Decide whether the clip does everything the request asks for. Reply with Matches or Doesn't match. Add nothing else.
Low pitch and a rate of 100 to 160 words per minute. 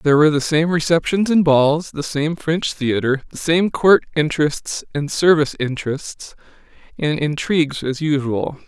Doesn't match